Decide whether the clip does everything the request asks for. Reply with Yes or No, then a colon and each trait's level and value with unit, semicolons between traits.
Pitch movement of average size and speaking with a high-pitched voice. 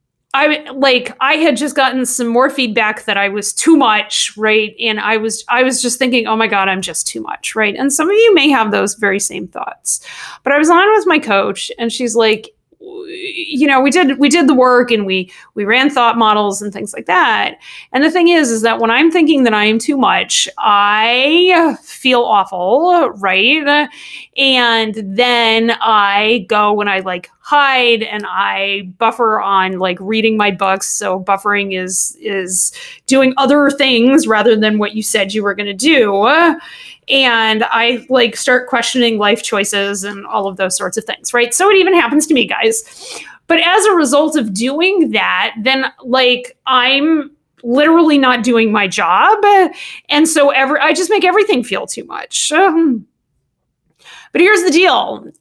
No: wide, 6.0 semitones; high, 245 Hz